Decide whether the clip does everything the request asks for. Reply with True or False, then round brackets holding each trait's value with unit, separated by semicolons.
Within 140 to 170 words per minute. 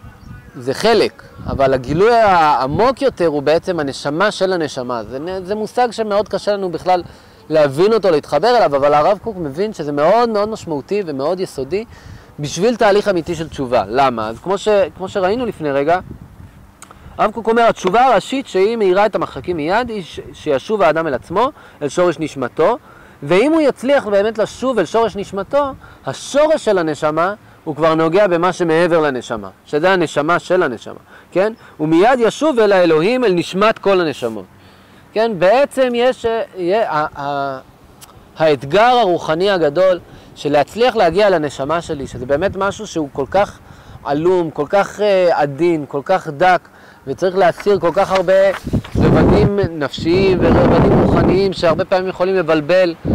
True (150 wpm)